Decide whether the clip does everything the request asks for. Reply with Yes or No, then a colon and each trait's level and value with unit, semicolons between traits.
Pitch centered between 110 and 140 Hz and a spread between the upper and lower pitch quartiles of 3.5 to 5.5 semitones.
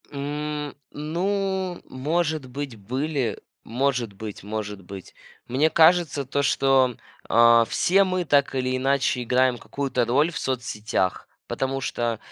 Yes: low, 135 Hz; average, 4.1 semitones